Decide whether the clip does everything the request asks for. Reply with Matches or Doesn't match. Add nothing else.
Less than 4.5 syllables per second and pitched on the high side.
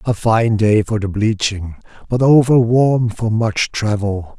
Doesn't match